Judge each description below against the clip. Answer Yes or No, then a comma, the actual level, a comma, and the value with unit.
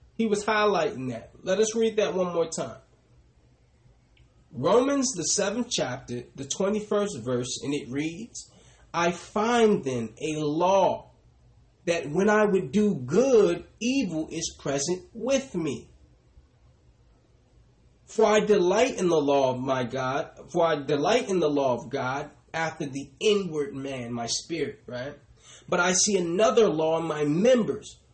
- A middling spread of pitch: No, wide, 7.2 semitones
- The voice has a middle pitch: Yes, medium, 165 Hz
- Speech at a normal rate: Yes, average, 150 wpm